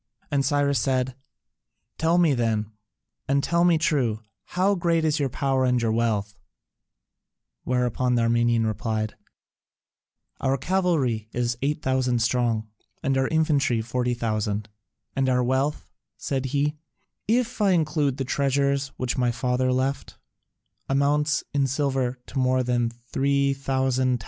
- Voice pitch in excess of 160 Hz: No, low, 130 Hz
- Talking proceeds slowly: Yes, slow, 130 wpm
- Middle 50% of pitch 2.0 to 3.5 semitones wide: Yes, average, 2.8 semitones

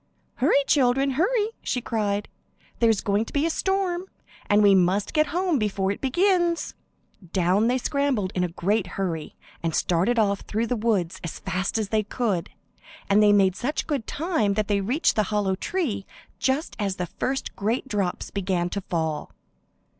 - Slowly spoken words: No, average, 175 wpm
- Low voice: No, high, 215 Hz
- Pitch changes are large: Yes, wide, 5.9 semitones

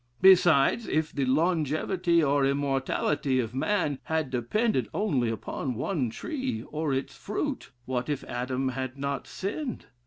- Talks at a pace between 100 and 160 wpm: Yes, slow, 135 wpm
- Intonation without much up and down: No, average, 5.0 semitones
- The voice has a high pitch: No, medium, 140 Hz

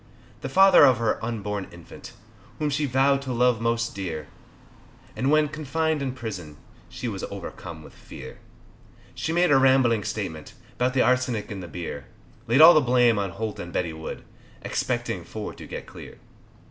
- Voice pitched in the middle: No, low, 120 Hz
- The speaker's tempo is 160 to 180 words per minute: Yes, average, 170 wpm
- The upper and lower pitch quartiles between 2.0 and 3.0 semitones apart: No, wide, 5.5 semitones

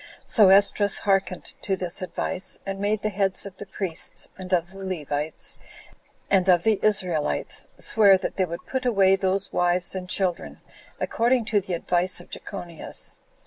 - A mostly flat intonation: Yes, narrow, 1.9 semitones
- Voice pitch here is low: No, high, 190 Hz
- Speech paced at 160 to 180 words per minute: Yes, average, 165 wpm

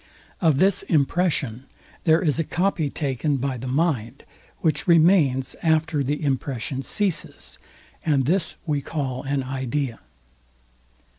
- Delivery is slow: Yes, slow, 125 wpm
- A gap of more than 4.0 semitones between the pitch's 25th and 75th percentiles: No, average, 3.6 semitones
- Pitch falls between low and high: Yes, medium, 145 Hz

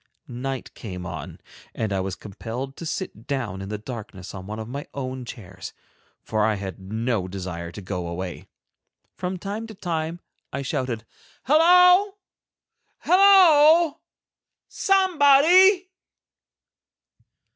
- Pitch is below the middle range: Yes, low, 130 Hz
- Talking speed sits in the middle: No, slow, 125 wpm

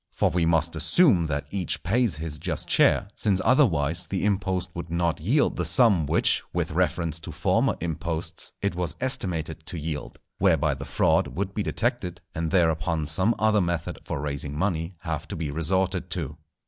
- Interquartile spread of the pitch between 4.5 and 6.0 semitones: No, average, 3.3 semitones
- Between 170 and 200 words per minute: Yes, average, 175 wpm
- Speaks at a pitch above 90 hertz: No, very low, 85 Hz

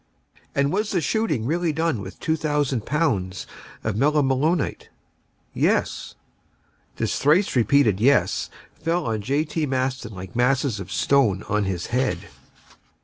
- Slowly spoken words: Yes, slow, 130 wpm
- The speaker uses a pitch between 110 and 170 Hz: Yes, low, 135 Hz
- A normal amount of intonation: No, wide, 5.8 semitones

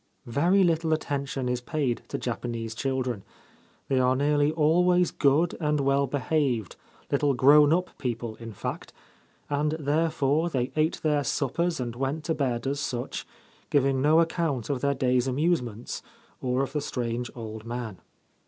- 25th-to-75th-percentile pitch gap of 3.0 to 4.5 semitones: Yes, average, 3.7 semitones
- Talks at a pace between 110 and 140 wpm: No, average, 155 wpm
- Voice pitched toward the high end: No, medium, 140 Hz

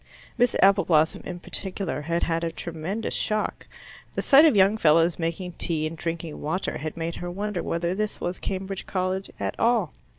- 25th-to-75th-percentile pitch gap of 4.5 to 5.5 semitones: No, average, 3.0 semitones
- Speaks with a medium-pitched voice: Yes, medium, 175 Hz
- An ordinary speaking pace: Yes, average, 175 wpm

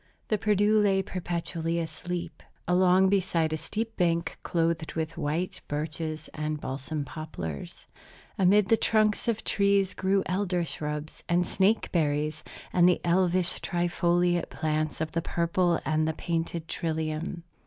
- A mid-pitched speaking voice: Yes, medium, 170 Hz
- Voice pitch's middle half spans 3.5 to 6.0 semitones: No, average, 2.9 semitones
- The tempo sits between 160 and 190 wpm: No, average, 140 wpm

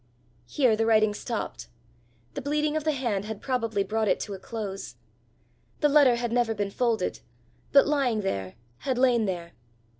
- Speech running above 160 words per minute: Yes, average, 170 wpm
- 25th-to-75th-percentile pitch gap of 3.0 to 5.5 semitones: Yes, average, 4.1 semitones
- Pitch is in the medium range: No, high, 230 Hz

